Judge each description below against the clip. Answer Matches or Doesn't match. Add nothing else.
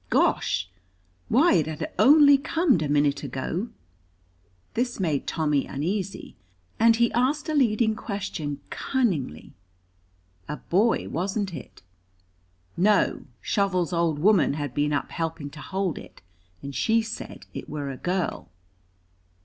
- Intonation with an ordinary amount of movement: Doesn't match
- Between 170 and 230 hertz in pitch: Matches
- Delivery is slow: Matches